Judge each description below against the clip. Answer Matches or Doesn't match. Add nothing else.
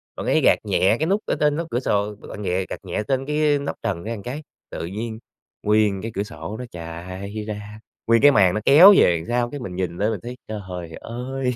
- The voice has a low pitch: Matches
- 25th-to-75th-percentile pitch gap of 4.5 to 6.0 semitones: Matches